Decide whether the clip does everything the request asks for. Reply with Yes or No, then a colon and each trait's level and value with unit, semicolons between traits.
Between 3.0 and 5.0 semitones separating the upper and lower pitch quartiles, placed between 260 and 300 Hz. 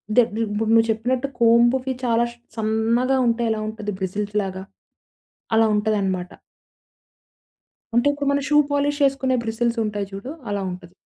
No: average, 3.4 semitones; high, 225 Hz